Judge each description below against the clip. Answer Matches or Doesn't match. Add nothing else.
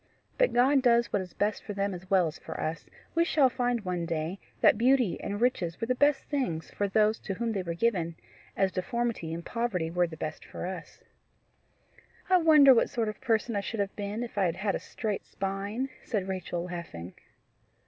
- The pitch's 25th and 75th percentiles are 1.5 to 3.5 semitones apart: Doesn't match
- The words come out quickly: Matches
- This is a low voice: Doesn't match